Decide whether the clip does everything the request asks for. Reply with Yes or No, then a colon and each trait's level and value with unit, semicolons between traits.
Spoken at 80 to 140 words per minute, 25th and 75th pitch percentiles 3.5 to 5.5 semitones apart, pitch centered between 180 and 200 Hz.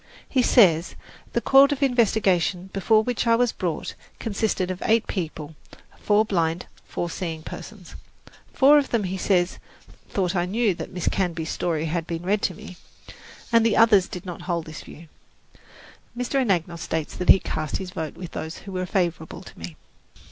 No: average, 175 wpm; average, 4.5 semitones; medium, 185 Hz